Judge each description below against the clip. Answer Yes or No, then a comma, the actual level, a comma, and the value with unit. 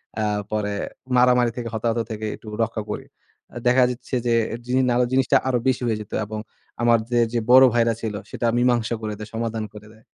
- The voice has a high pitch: No, low, 115 Hz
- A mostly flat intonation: Yes, narrow, 2.1 semitones